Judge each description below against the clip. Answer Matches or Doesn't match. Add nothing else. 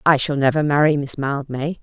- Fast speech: Doesn't match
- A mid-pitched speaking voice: Matches